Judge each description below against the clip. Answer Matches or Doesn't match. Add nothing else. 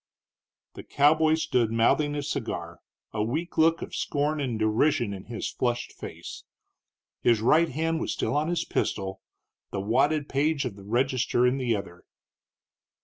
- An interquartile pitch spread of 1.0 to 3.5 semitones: Doesn't match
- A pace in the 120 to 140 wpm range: Doesn't match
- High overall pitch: Doesn't match